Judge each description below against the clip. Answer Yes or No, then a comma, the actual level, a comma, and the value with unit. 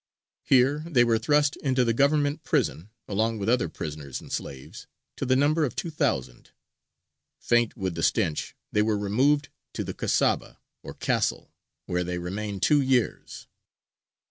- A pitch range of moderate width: No, wide, 6.8 semitones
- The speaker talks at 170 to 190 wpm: No, average, 155 wpm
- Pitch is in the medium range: No, low, 115 Hz